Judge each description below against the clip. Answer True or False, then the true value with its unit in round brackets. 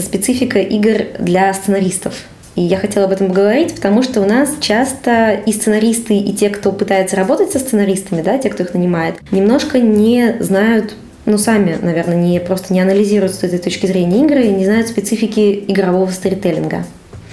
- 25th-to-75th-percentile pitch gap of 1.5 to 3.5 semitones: True (2.8 semitones)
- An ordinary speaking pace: False (175 wpm)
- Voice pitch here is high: True (200 Hz)